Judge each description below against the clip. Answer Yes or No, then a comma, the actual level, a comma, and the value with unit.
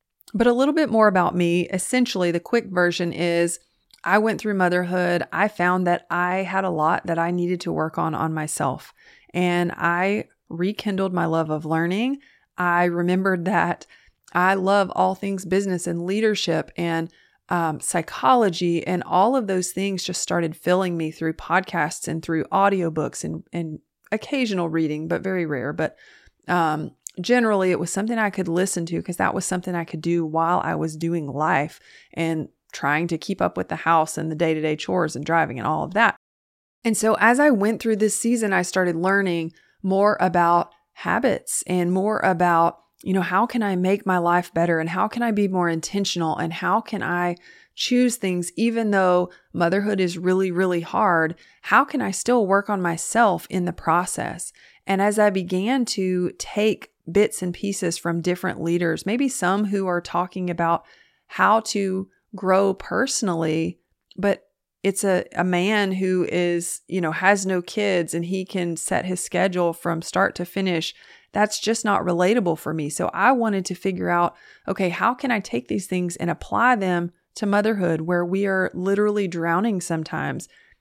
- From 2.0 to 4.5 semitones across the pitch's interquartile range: Yes, average, 2.9 semitones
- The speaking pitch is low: No, medium, 180 Hz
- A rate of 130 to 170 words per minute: No, average, 180 wpm